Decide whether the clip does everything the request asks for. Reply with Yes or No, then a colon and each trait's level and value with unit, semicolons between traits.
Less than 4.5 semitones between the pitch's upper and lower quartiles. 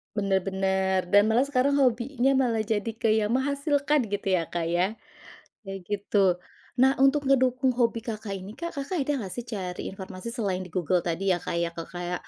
No: average, 5.2 semitones